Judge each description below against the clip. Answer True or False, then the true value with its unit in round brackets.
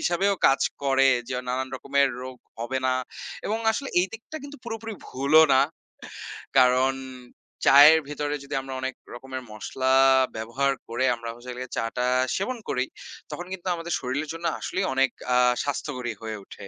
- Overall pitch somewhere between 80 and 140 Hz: True (135 Hz)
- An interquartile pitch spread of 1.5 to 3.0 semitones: False (4.0 semitones)